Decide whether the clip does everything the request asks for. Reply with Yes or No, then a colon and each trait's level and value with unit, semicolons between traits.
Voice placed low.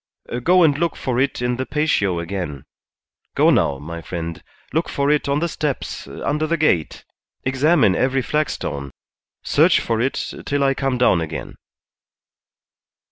Yes: low, 130 Hz